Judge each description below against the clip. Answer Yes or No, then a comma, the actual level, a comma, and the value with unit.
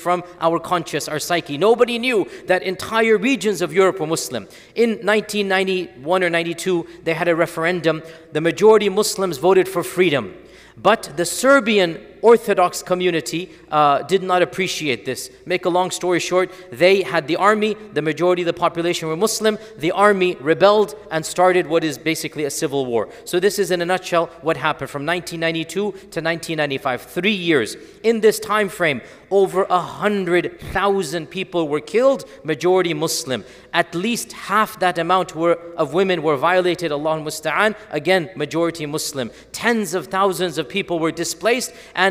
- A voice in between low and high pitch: Yes, medium, 180 Hz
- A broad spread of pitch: No, average, 3.2 semitones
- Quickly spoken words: No, average, 165 wpm